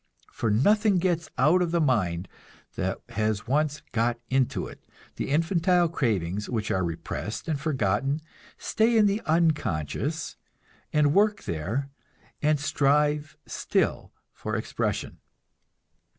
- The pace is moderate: No, slow, 120 wpm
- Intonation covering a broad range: Yes, wide, 7.1 semitones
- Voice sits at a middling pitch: Yes, medium, 145 Hz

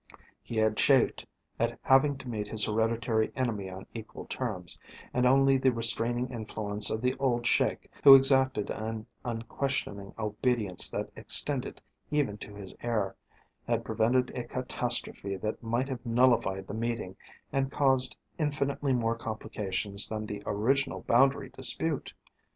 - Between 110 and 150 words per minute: Yes, average, 140 wpm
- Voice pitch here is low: Yes, low, 115 Hz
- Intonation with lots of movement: No, average, 3.4 semitones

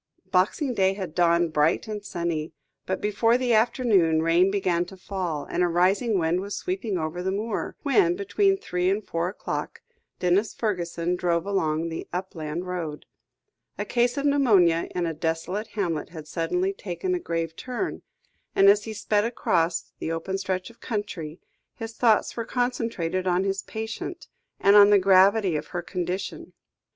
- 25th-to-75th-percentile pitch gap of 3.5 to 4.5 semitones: Yes, average, 4.0 semitones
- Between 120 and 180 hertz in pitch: No, high, 190 Hz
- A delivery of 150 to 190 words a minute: Yes, average, 165 wpm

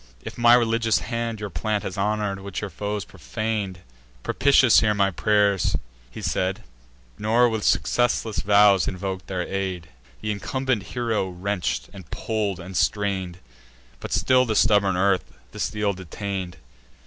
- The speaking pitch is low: Yes, low, 100 Hz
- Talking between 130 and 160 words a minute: Yes, average, 150 wpm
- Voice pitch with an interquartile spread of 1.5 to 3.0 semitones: Yes, narrow, 2.6 semitones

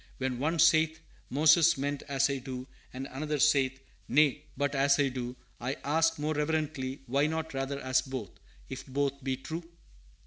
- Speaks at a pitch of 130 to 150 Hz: Yes, medium, 140 Hz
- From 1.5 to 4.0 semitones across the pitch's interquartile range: Yes, narrow, 2.5 semitones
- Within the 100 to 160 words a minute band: No, average, 170 wpm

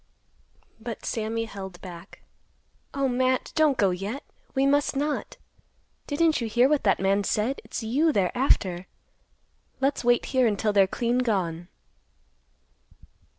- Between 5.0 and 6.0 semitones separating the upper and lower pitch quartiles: Yes, wide, 5.5 semitones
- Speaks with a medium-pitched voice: No, high, 235 Hz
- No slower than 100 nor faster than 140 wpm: Yes, slow, 135 wpm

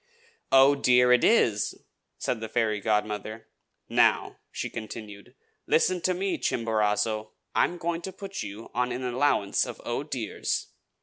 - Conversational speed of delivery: Yes, average, 145 wpm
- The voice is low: Yes, low, 120 Hz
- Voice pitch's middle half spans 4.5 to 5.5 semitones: Yes, average, 5.1 semitones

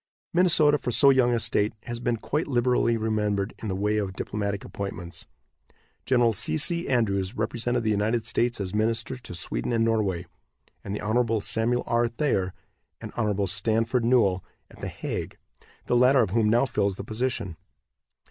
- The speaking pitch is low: Yes, low, 115 Hz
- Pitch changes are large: No, average, 3.1 semitones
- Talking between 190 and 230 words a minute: No, average, 170 wpm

